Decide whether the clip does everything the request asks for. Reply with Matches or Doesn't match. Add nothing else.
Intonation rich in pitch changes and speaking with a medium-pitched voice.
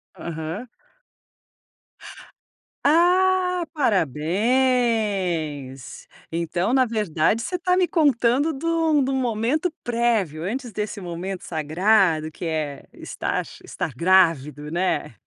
Doesn't match